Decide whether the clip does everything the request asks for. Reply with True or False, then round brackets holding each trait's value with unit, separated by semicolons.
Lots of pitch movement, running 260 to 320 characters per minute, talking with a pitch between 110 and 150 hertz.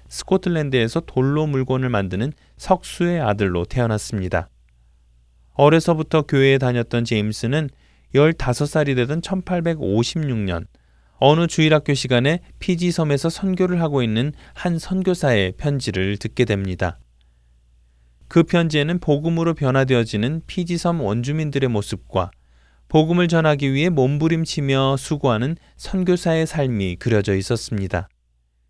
True (8.1 semitones; 290 characters per minute; 135 Hz)